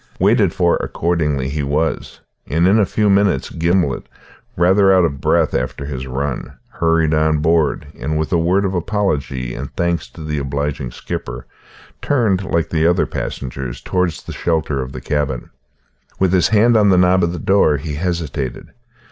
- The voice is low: Yes, very low, 80 Hz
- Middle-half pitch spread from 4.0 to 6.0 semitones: Yes, average, 4.5 semitones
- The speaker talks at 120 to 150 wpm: No, average, 175 wpm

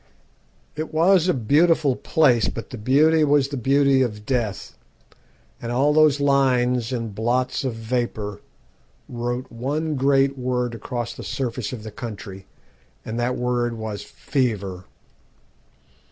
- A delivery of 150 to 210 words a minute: No, slow, 135 wpm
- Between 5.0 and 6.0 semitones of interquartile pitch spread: No, average, 3.3 semitones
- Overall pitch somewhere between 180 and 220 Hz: No, low, 125 Hz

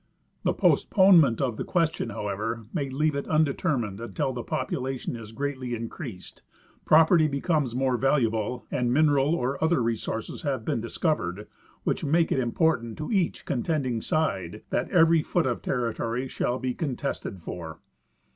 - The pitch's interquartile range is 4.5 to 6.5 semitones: Yes, average, 5.1 semitones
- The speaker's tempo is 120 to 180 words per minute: Yes, average, 150 wpm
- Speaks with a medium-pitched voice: No, low, 130 Hz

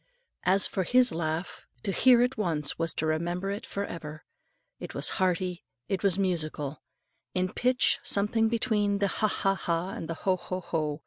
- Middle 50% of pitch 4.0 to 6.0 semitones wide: No, average, 3.5 semitones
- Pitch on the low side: No, medium, 185 Hz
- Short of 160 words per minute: No, average, 180 wpm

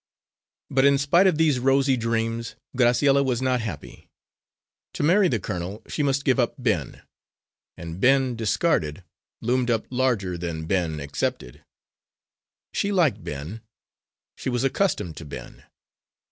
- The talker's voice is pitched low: Yes, low, 120 Hz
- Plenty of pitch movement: Yes, wide, 6.6 semitones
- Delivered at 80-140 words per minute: Yes, slow, 135 wpm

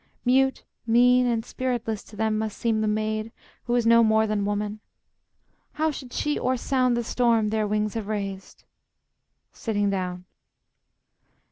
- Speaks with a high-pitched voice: Yes, high, 220 Hz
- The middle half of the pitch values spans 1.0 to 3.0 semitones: Yes, narrow, 2.5 semitones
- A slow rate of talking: No, average, 150 wpm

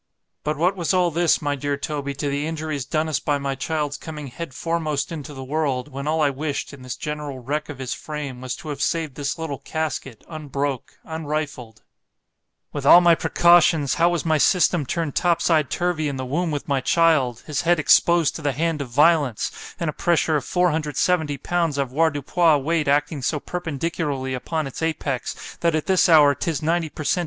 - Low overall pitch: No, medium, 150 Hz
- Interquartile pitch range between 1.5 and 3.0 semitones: Yes, average, 2.7 semitones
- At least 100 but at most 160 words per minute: No, average, 195 wpm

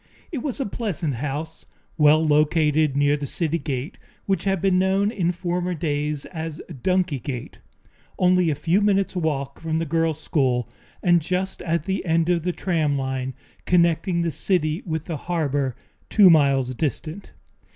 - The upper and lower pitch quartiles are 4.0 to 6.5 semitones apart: No, average, 3.6 semitones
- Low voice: No, medium, 160 Hz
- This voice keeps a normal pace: Yes, average, 160 wpm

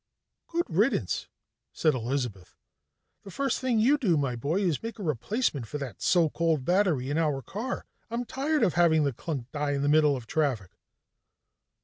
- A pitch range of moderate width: No, wide, 6.8 semitones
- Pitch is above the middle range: No, medium, 155 Hz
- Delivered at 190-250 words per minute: No, average, 175 wpm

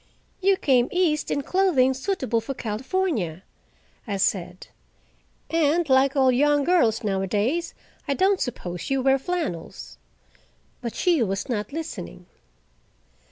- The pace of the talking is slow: Yes, slow, 120 wpm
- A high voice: Yes, very high, 270 Hz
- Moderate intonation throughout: No, wide, 7.1 semitones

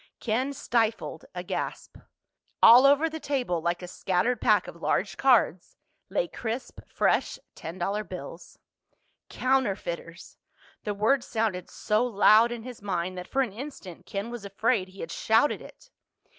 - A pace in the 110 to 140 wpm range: No, average, 150 wpm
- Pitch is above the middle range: Yes, high, 220 Hz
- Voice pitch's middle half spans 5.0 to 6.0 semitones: Yes, wide, 5.4 semitones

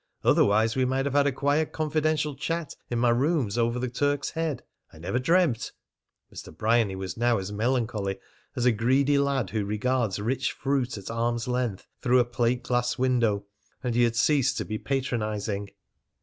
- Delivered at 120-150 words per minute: No, average, 180 wpm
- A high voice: No, low, 120 Hz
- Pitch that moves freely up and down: No, average, 3.6 semitones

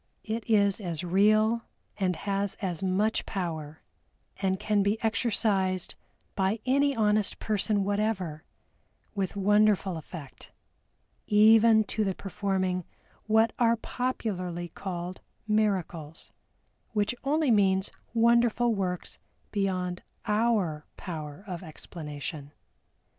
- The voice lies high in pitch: Yes, high, 200 Hz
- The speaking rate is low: Yes, slow, 105 wpm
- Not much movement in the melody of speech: No, average, 3.2 semitones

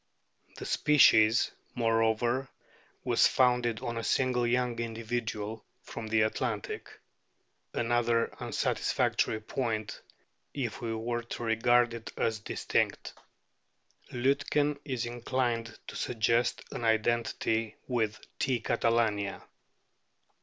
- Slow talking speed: Yes, slow, 105 wpm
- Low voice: Yes, low, 115 Hz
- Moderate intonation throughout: No, narrow, 1.5 semitones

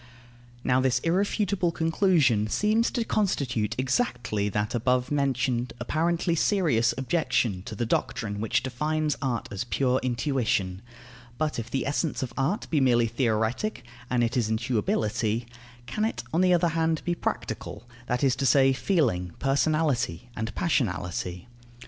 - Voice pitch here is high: No, low, 130 Hz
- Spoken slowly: No, average, 145 wpm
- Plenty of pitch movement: Yes, wide, 5.8 semitones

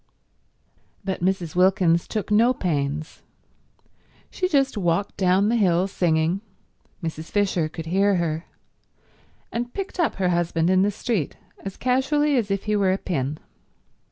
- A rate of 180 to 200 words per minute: No, slow, 135 wpm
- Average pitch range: Yes, average, 3.9 semitones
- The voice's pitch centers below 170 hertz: No, high, 190 Hz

